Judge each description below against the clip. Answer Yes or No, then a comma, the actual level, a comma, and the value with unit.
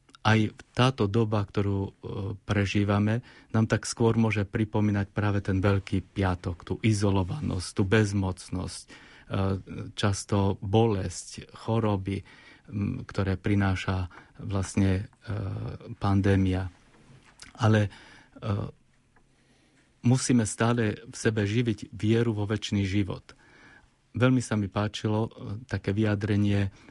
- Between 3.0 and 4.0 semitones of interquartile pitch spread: No, narrow, 2.5 semitones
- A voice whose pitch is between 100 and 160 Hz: Yes, low, 105 Hz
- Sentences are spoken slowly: Yes, slow, 90 wpm